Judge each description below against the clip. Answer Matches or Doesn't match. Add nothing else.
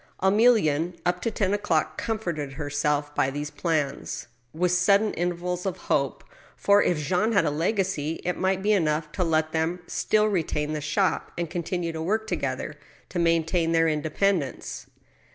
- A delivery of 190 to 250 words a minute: Doesn't match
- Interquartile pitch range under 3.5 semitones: Doesn't match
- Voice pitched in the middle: Matches